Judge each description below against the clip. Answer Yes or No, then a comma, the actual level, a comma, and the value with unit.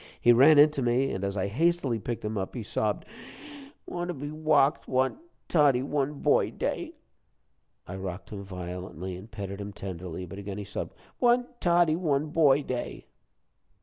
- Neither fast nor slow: Yes, average, 175 wpm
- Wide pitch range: Yes, wide, 7.2 semitones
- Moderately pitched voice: No, low, 125 Hz